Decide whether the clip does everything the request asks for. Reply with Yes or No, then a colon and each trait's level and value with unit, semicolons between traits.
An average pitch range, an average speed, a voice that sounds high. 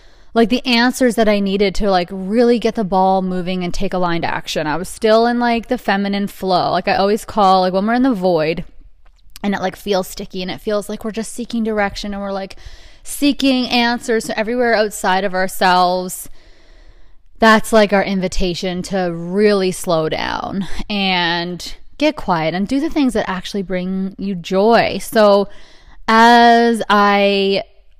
Yes: average, 3.3 semitones; average, 175 wpm; high, 200 Hz